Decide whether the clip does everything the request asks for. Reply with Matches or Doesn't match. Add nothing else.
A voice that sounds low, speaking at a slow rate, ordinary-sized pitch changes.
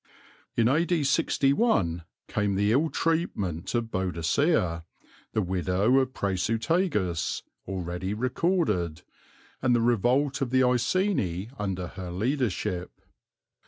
Doesn't match